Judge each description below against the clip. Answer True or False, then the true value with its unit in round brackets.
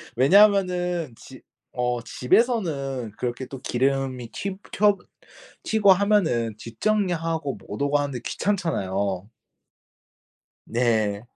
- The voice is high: False (140 Hz)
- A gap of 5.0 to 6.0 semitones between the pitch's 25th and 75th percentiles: False (7.9 semitones)